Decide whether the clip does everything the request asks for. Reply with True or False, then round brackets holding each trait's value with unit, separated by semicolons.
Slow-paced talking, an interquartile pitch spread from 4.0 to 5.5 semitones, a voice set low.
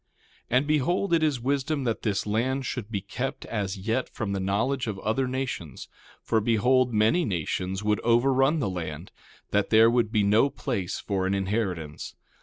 False (180 wpm; 4.8 semitones; 115 Hz)